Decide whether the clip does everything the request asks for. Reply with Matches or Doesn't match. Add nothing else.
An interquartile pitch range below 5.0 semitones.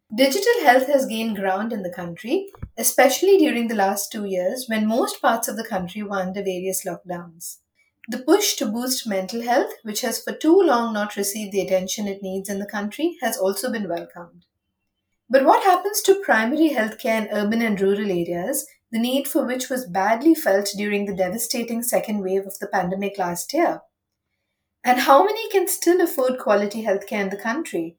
Doesn't match